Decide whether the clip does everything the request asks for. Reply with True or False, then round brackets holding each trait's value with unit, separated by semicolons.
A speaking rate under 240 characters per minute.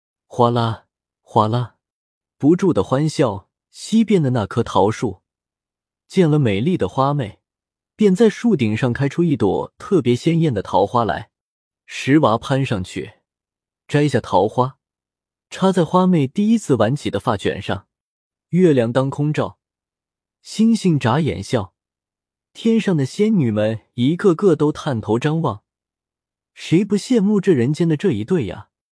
True (205 characters per minute)